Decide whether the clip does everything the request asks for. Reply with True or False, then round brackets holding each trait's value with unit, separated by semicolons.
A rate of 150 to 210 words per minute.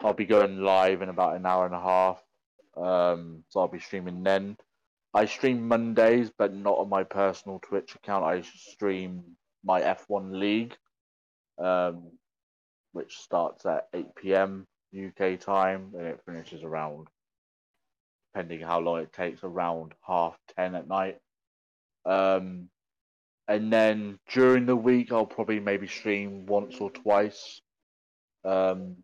False (140 wpm)